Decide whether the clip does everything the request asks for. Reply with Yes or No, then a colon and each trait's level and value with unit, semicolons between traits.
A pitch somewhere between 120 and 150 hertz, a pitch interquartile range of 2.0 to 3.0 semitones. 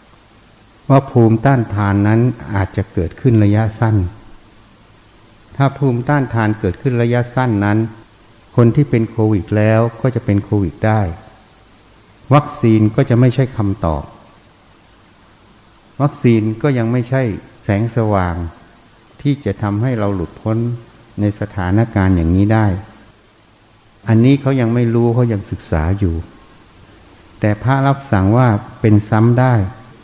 No: low, 110 Hz; average, 2.7 semitones